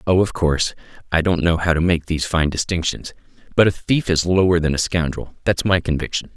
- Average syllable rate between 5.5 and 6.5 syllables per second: Yes, 5.8 syllables/s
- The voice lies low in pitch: Yes, very low, 85 Hz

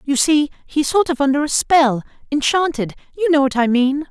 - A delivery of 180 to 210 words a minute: Yes, fast, 205 wpm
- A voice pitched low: No, very high, 285 Hz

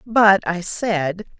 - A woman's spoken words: Yes, female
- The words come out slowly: Yes, slow, 130 wpm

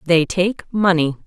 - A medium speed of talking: Yes, average, 145 wpm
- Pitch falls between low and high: Yes, medium, 180 Hz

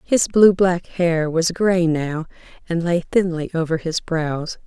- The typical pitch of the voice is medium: Yes, medium, 170 Hz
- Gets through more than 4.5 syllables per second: No, 3.8 syllables/s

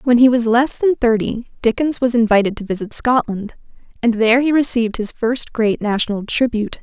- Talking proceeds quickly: No, average, 185 wpm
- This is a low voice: No, high, 235 Hz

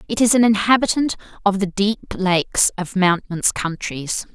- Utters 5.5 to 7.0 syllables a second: No, 4.9 syllables/s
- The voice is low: No, high, 200 Hz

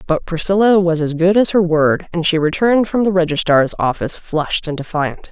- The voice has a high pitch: No, medium, 170 Hz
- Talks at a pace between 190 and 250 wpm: Yes, fast, 205 wpm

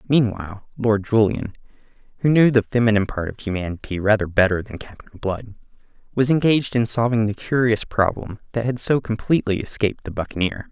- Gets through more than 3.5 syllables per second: Yes, 5.9 syllables/s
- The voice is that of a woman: No, male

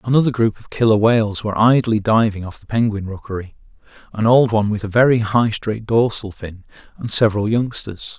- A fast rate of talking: No, average, 185 wpm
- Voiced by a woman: No, male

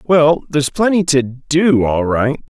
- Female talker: No, male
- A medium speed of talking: Yes, average, 160 wpm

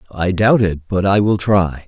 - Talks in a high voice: No, very low, 95 Hz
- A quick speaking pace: Yes, fast, 225 wpm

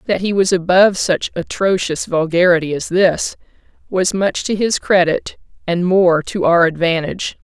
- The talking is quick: No, average, 155 wpm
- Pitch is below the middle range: No, medium, 180 Hz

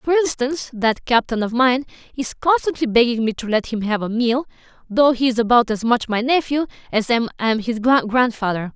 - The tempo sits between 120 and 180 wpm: No, average, 190 wpm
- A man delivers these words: No, female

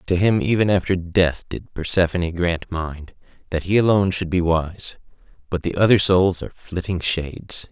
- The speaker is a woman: No, male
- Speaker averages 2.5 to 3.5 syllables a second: Yes, 3.3 syllables/s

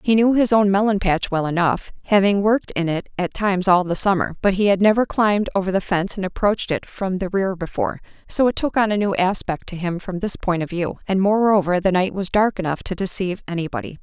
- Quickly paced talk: Yes, fast, 240 wpm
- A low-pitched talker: No, high, 190 Hz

